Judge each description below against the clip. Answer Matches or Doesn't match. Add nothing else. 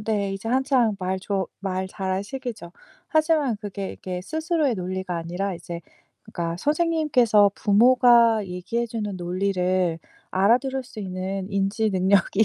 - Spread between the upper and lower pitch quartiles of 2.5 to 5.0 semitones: Matches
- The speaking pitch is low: Doesn't match